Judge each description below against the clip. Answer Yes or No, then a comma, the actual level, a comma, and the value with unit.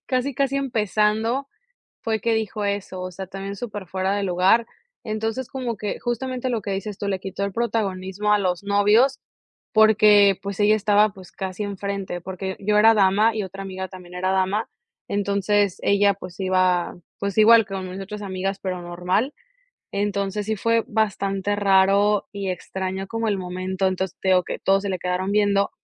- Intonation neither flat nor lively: No, narrow, 2.1 semitones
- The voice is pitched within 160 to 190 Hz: No, high, 200 Hz